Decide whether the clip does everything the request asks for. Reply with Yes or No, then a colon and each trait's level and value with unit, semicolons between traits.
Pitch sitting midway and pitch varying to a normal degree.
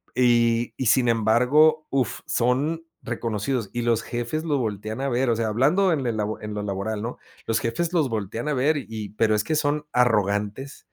No: low, 120 Hz; average, 4.1 semitones